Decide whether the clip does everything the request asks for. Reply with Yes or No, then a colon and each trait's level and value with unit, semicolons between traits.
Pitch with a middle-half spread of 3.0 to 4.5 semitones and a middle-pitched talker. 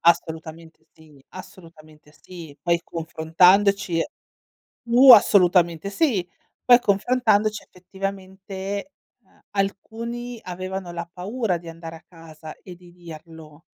Yes: average, 3.5 semitones; medium, 180 Hz